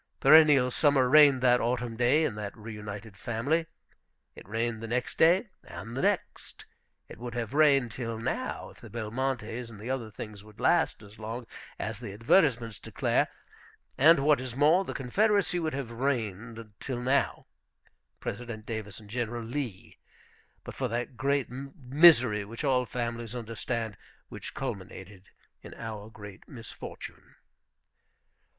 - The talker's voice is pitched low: Yes, low, 120 Hz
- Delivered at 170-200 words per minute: No, average, 145 wpm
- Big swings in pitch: No, average, 3.5 semitones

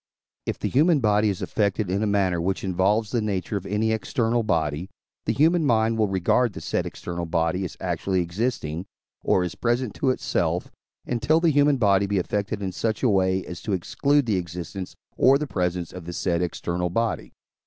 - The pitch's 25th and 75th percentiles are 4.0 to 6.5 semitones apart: Yes, average, 4.3 semitones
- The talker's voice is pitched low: Yes, low, 100 Hz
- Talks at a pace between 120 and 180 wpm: No, average, 195 wpm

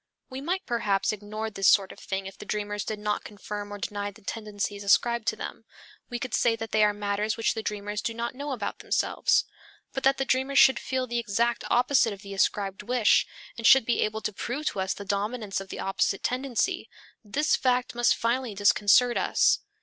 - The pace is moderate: No, fast, 210 wpm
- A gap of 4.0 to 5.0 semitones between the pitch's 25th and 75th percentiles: No, average, 3.2 semitones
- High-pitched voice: Yes, high, 220 Hz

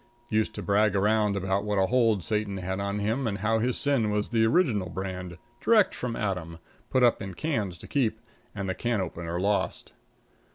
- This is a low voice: Yes, low, 105 Hz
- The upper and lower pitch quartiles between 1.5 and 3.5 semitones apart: Yes, average, 2.9 semitones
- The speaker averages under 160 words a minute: No, average, 195 wpm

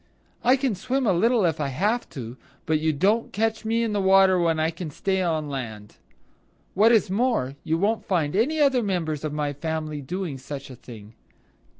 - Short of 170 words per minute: No, average, 200 wpm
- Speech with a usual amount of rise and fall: No, wide, 6.6 semitones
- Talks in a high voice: No, medium, 175 Hz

